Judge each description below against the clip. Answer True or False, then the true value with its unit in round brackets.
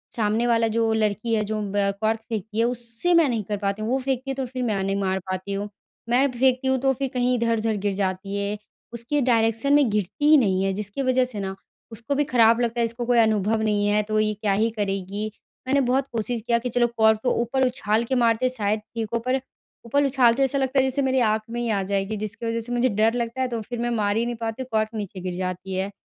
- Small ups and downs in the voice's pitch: False (3.2 semitones)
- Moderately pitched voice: False (230 Hz)